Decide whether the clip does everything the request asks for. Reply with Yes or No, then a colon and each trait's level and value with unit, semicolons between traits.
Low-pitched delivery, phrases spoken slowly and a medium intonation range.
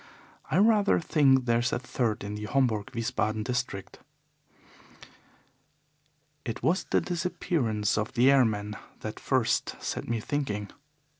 Yes: low, 120 Hz; slow, 130 wpm; average, 4.5 semitones